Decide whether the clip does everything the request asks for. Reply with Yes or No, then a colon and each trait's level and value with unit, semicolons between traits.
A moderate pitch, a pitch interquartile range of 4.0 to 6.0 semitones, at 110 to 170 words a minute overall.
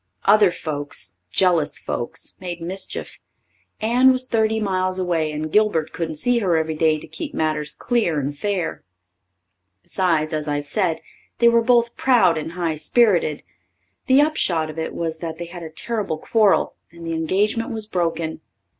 Yes: medium, 175 Hz; average, 5.2 semitones; average, 160 wpm